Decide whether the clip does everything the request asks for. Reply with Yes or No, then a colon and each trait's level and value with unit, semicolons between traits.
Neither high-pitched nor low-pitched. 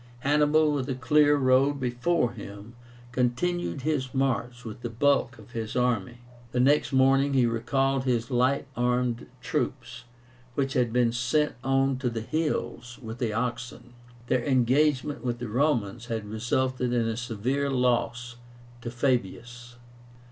No: low, 125 Hz